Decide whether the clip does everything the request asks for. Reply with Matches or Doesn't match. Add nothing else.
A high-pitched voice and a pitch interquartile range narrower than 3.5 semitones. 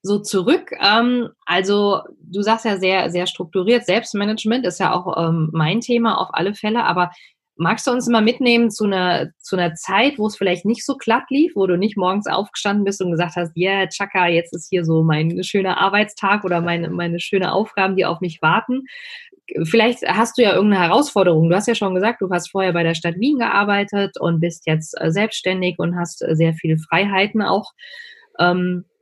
Doesn't match